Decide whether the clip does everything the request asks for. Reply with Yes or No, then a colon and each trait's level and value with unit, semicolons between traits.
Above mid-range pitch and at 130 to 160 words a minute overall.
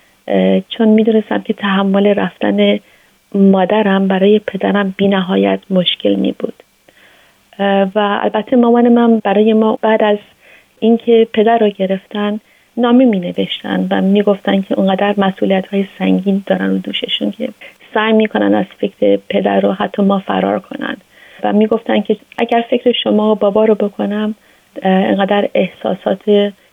Yes: high, 205 Hz; average, 145 wpm